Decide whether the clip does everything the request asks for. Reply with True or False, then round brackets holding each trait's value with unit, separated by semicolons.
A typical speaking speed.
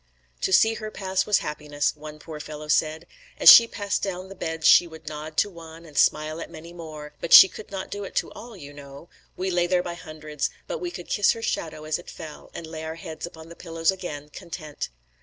False (235 wpm)